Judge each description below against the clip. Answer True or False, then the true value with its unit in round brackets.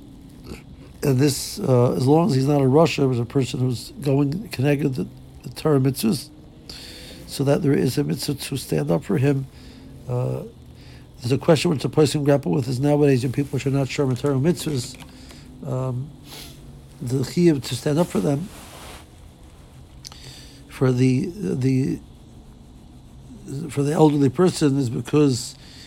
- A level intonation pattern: True (2.2 semitones)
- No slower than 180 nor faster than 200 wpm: False (155 wpm)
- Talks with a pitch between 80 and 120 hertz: False (140 Hz)